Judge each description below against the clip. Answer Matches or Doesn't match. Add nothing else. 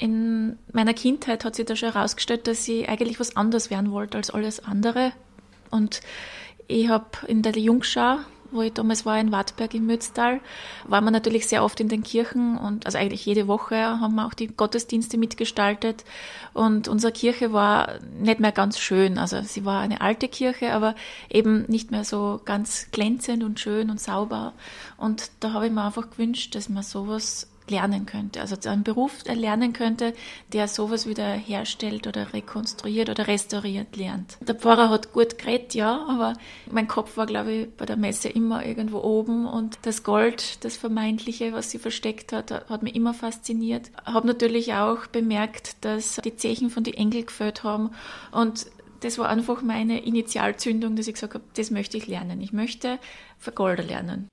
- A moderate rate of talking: Matches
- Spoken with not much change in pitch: Matches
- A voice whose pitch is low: Doesn't match